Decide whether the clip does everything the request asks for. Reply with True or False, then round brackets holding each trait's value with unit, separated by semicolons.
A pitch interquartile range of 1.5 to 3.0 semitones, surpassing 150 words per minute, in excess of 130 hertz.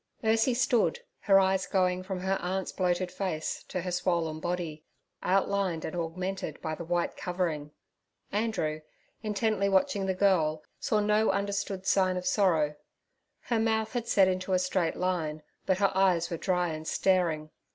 True (2.6 semitones; 160 wpm; 185 Hz)